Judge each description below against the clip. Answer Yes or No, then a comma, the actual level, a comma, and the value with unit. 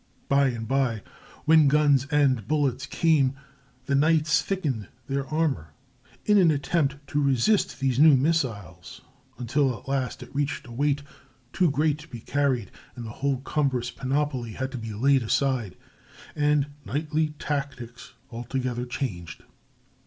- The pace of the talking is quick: No, average, 145 wpm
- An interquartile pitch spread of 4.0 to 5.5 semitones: No, average, 3.1 semitones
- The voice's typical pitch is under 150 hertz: Yes, medium, 140 Hz